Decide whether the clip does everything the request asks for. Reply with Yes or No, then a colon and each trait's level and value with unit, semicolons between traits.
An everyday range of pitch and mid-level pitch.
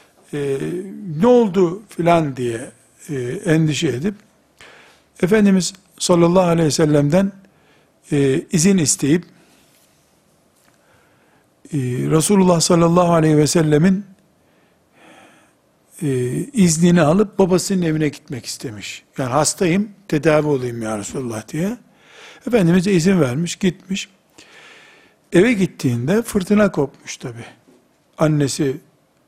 Yes: average, 4.4 semitones; medium, 170 Hz